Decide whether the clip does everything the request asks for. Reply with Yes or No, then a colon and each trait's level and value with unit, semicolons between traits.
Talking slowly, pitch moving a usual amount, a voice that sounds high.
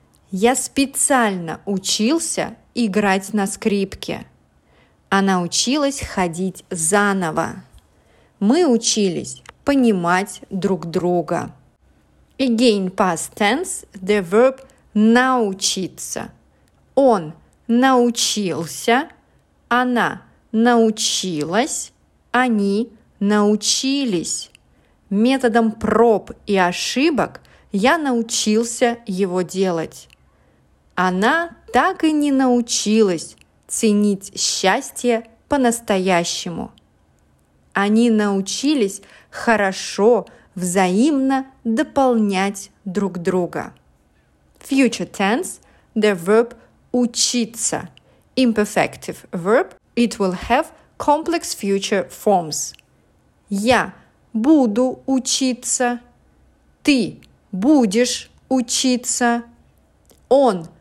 Yes: slow, 70 wpm; average, 4.5 semitones; high, 220 Hz